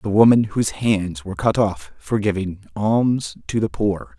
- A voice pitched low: Yes, low, 105 Hz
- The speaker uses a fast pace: No, average, 185 wpm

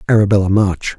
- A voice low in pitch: Yes, low, 100 Hz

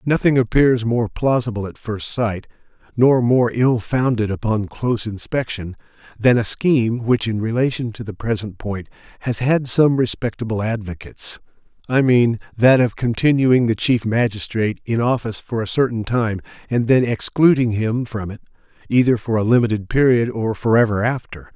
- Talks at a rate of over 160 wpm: No, average, 155 wpm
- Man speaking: Yes, male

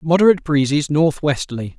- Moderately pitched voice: Yes, medium, 150 Hz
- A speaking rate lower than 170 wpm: Yes, slow, 135 wpm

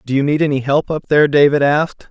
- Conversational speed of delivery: No, fast, 255 wpm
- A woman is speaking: No, male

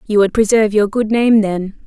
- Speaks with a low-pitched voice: No, high, 210 Hz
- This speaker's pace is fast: Yes, fast, 225 wpm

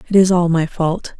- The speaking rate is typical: No, fast, 250 wpm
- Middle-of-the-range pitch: Yes, medium, 175 Hz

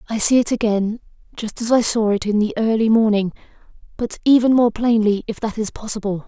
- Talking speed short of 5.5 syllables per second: No, 5.7 syllables/s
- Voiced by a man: No, female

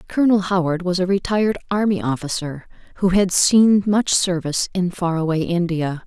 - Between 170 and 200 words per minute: No, average, 160 wpm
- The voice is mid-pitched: Yes, medium, 180 Hz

